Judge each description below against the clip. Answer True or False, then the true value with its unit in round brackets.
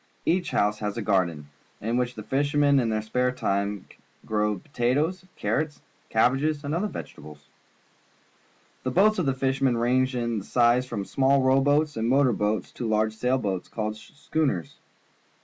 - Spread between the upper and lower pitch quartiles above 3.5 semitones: True (4.6 semitones)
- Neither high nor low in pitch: False (125 Hz)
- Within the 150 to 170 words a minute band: True (160 wpm)